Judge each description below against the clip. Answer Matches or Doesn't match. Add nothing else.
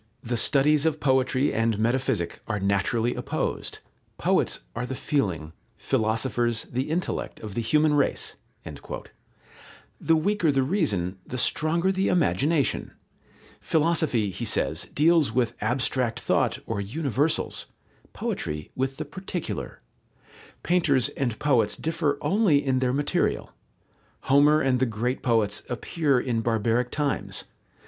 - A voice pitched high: Doesn't match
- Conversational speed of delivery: Doesn't match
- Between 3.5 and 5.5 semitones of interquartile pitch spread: Matches